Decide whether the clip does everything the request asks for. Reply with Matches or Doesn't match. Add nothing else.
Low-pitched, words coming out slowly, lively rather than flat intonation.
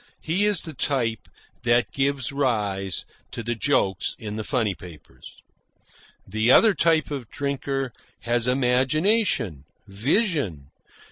Doesn't match